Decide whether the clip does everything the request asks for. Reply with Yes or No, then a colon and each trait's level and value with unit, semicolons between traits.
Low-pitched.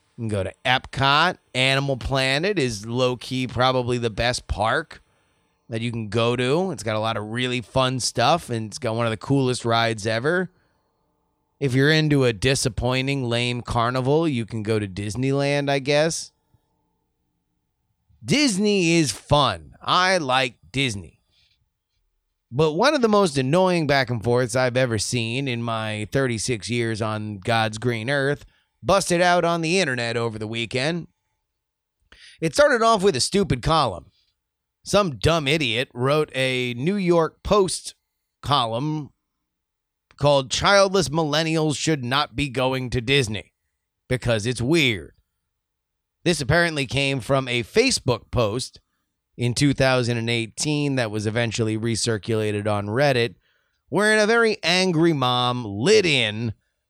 Yes: low, 130 Hz